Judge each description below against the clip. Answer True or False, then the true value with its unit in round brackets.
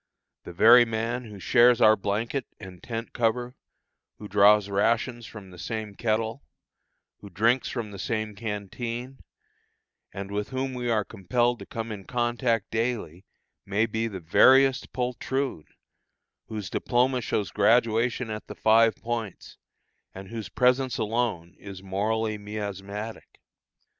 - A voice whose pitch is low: True (110 Hz)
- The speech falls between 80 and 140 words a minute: True (135 wpm)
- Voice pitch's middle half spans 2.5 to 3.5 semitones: True (2.9 semitones)